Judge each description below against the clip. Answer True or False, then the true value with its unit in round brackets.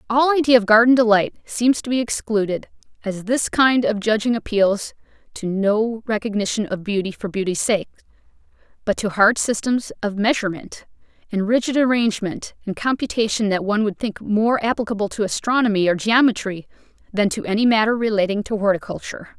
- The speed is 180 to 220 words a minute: False (160 wpm)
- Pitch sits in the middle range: False (220 Hz)